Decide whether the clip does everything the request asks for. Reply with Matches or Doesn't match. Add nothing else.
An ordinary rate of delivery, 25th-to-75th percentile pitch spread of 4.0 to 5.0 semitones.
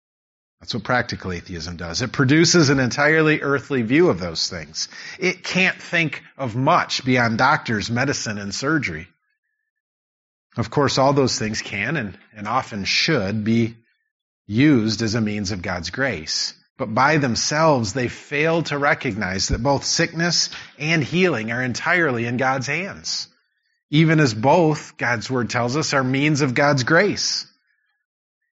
Doesn't match